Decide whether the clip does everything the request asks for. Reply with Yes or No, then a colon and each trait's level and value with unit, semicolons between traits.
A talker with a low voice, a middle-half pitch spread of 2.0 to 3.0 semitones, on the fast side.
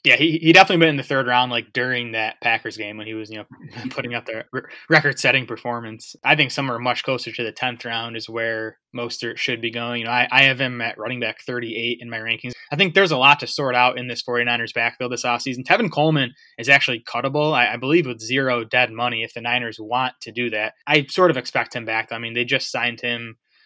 Yes: low, 120 Hz; narrow, 2.5 semitones; fast, 250 wpm